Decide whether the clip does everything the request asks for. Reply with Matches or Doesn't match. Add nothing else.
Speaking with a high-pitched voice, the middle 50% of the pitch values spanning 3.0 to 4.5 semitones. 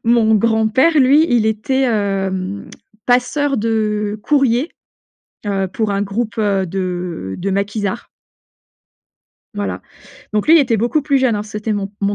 Matches